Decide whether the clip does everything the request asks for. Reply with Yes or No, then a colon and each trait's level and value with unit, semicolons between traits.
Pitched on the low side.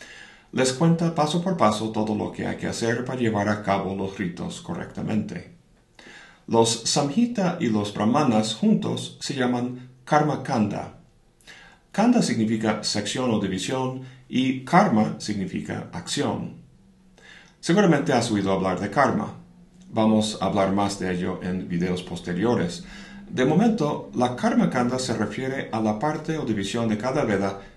Yes: low, 125 Hz